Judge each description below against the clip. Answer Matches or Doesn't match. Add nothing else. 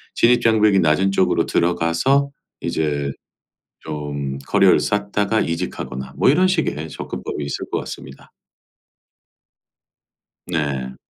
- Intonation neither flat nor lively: Doesn't match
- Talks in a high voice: Doesn't match